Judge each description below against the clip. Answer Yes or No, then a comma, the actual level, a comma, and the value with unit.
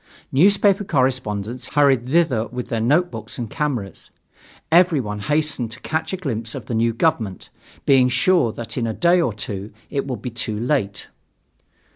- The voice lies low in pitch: Yes, low, 125 Hz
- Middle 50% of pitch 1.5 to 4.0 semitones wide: No, average, 5.3 semitones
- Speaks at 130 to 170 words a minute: Yes, average, 160 wpm